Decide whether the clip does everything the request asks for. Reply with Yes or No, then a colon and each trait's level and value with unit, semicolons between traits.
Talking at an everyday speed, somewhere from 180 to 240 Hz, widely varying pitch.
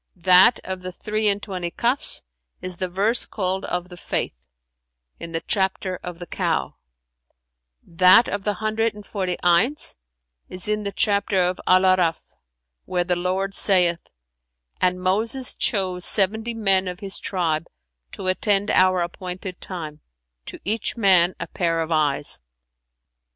No: average, 150 wpm; medium, 185 Hz; narrow, 2.5 semitones